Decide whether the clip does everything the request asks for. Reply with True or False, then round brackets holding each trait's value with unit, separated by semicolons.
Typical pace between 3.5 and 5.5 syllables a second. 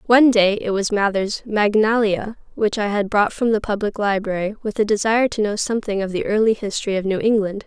False (5.8 syllables/s)